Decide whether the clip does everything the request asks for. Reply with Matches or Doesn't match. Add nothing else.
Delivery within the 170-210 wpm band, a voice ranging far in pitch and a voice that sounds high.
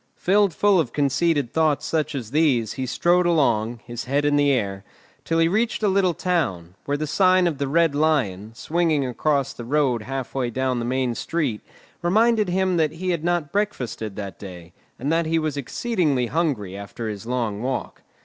Doesn't match